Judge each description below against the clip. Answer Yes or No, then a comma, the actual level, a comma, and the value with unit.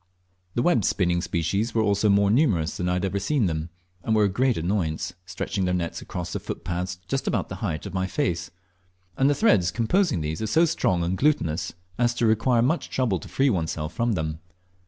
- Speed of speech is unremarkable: No, fast, 210 wpm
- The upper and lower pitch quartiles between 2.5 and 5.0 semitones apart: No, wide, 5.4 semitones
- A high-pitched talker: No, low, 100 Hz